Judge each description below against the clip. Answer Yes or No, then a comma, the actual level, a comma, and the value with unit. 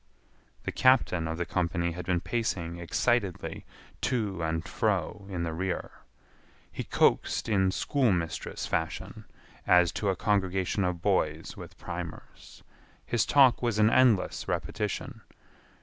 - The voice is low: Yes, very low, 95 Hz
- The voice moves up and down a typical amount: Yes, average, 4.0 semitones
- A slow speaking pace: Yes, slow, 130 wpm